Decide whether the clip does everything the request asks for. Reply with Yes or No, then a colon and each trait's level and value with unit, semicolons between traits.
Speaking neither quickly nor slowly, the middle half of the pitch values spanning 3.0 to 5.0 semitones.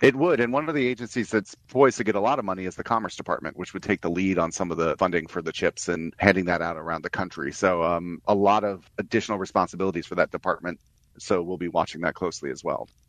No: fast, 260 wpm; average, 4.2 semitones